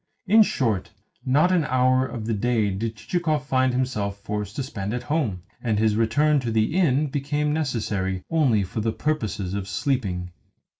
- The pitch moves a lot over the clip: Yes, wide, 5.7 semitones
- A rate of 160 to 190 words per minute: Yes, average, 170 wpm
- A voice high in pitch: No, low, 120 Hz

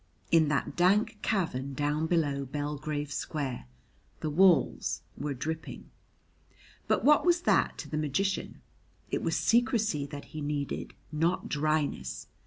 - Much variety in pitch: No, average, 3.8 semitones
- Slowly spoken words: Yes, slow, 130 wpm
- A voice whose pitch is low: No, medium, 150 Hz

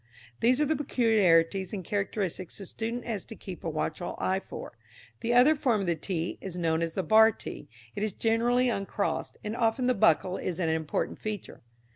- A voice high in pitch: Yes, high, 200 Hz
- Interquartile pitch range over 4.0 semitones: Yes, average, 4.8 semitones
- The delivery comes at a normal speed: Yes, average, 195 wpm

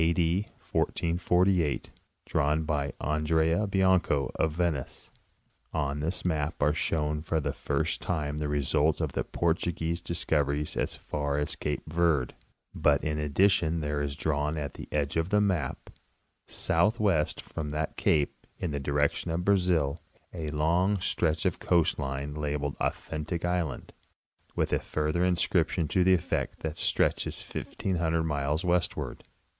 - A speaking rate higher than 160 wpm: No, average, 145 wpm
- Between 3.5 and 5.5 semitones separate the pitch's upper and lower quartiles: No, average, 2.8 semitones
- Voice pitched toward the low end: Yes, very low, 80 Hz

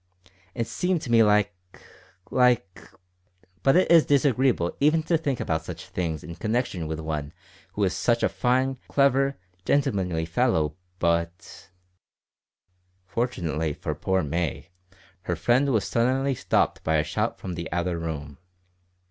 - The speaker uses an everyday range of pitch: No, wide, 7.5 semitones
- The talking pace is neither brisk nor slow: Yes, average, 145 wpm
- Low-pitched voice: Yes, very low, 95 Hz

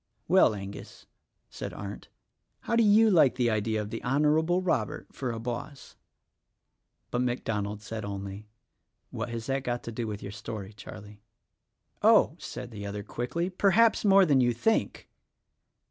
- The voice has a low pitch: Yes, low, 120 Hz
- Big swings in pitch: Yes, wide, 6.4 semitones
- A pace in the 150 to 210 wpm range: Yes, average, 155 wpm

